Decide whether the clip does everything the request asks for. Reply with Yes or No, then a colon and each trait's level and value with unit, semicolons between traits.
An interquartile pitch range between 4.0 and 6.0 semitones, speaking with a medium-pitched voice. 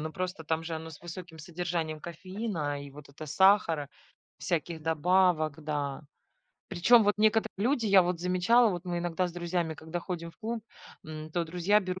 No: average, 2.8 semitones; medium, 175 Hz